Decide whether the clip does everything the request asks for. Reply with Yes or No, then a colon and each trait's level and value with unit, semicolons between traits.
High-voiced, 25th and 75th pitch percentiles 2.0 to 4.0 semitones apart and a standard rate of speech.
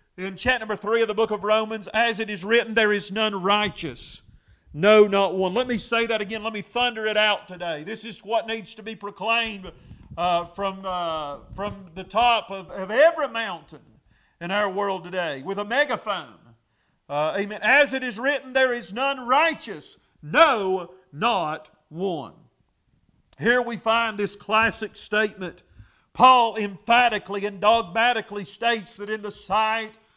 Yes: high, 210 Hz; average, 3.3 semitones; average, 165 wpm